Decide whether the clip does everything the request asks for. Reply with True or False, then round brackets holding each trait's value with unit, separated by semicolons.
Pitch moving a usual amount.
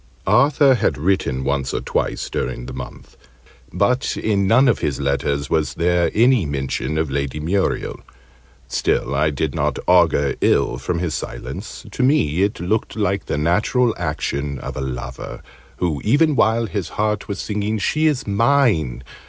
False (7.7 semitones)